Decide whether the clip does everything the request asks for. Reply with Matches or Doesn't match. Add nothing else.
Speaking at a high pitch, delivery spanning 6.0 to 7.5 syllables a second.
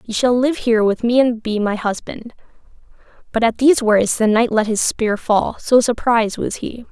Doesn't match